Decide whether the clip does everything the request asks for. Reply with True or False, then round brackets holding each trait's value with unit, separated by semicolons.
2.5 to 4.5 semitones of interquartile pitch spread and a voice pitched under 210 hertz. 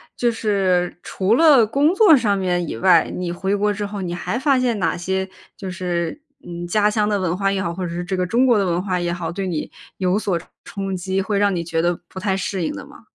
True (2.8 semitones; 190 Hz)